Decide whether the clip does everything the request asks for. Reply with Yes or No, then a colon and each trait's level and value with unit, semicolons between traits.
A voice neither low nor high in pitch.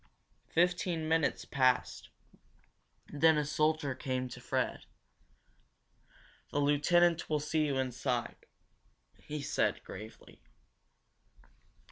Yes: medium, 150 Hz